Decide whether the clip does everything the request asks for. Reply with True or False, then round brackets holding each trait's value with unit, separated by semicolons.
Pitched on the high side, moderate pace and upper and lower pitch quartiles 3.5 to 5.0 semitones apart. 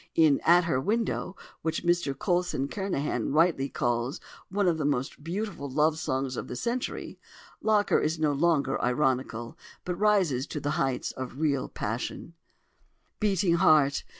False (155 Hz; 150 wpm; 4.6 semitones)